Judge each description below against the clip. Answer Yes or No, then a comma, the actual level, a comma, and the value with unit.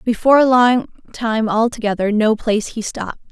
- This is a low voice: No, high, 225 Hz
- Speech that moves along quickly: No, average, 145 wpm